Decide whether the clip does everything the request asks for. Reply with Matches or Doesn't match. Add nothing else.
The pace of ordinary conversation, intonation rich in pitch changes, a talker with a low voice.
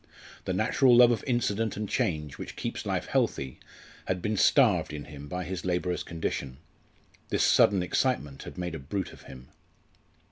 Matches